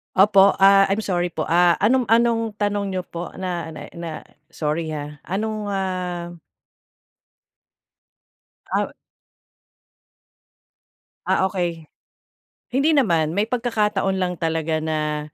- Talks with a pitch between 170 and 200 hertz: Yes, medium, 185 Hz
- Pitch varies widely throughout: No, average, 4.0 semitones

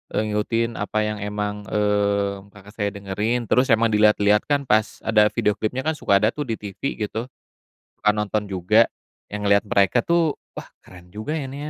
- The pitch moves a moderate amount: No, narrow, 2.1 semitones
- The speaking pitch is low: Yes, low, 105 Hz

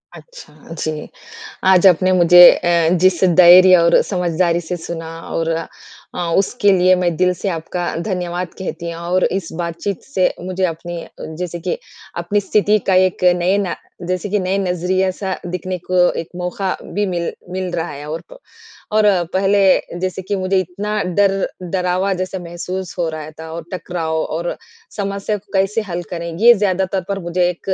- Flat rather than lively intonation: Yes, narrow, 1.8 semitones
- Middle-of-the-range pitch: Yes, medium, 180 Hz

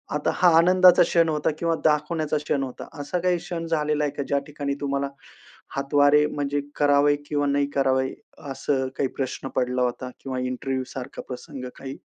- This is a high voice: No, medium, 145 Hz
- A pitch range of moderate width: No, narrow, 2.1 semitones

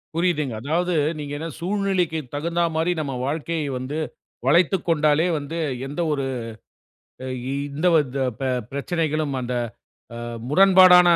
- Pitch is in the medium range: Yes, medium, 160 Hz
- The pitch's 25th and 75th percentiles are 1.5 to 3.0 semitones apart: No, average, 3.4 semitones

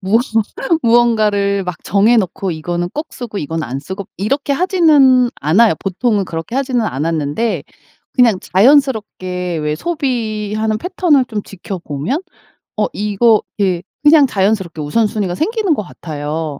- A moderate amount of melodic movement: No, wide, 5.8 semitones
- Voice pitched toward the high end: Yes, high, 210 Hz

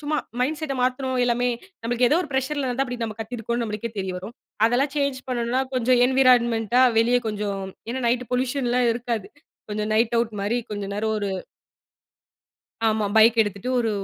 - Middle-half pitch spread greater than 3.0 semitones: No, narrow, 2.6 semitones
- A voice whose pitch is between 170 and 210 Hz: No, high, 240 Hz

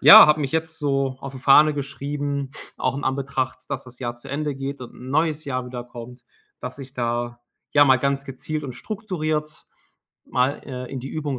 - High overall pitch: No, low, 135 Hz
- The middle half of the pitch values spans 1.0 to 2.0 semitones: No, narrow, 2.6 semitones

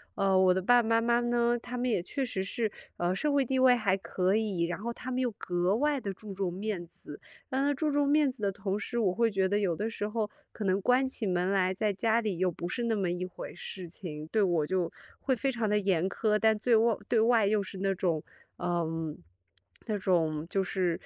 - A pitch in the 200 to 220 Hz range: Yes, high, 205 Hz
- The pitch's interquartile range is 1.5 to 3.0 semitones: No, average, 4.4 semitones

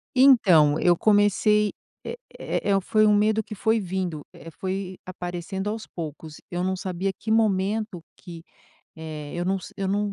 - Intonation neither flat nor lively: Yes, average, 3.3 semitones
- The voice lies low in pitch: No, high, 190 Hz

